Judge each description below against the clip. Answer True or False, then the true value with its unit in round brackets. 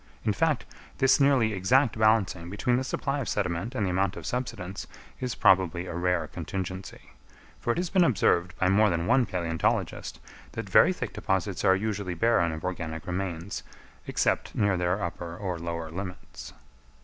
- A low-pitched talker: True (95 Hz)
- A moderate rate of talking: True (170 wpm)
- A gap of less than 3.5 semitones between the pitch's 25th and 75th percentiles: False (4.1 semitones)